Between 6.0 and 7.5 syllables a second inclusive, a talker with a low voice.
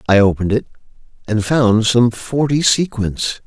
No: 4.5 syllables/s; low, 120 Hz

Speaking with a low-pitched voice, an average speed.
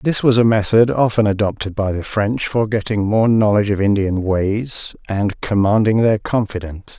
Yes: low, 105 Hz; average, 170 wpm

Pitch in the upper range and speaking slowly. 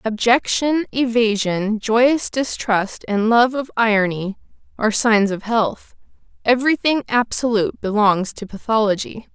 Yes: high, 225 Hz; slow, 110 wpm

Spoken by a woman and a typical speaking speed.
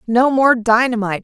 Yes: female; average, 145 wpm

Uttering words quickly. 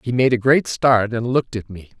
Yes: fast, 270 wpm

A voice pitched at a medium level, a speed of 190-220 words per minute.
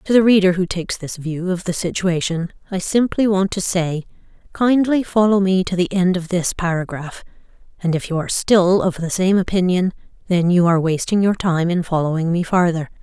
Yes: medium, 180 Hz; average, 200 wpm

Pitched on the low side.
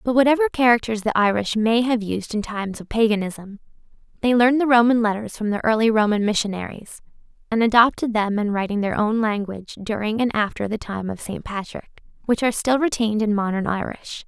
No: high, 220 Hz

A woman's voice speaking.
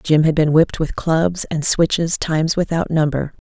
Yes: female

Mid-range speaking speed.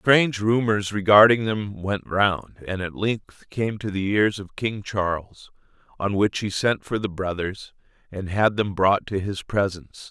Yes: average, 180 wpm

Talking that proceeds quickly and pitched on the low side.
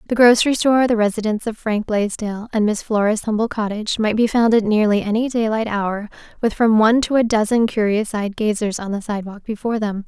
No: fast, 210 wpm; high, 220 Hz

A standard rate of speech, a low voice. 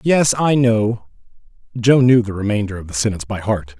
Yes: average, 190 wpm; low, 110 Hz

